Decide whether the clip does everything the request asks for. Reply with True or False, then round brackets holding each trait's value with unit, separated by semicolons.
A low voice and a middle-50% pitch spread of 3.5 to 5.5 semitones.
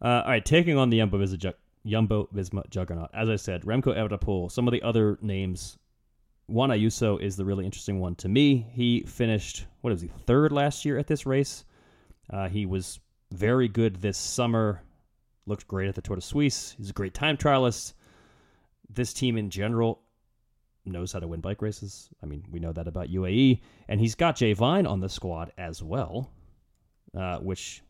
True (105 Hz; 4.2 semitones)